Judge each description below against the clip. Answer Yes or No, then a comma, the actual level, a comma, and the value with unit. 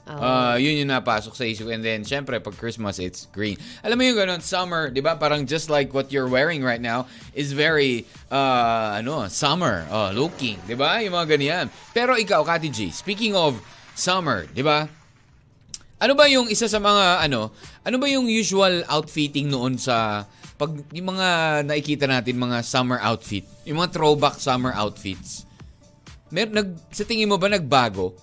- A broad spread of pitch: Yes, wide, 6.6 semitones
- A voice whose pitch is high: No, medium, 145 Hz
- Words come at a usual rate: No, fast, 175 wpm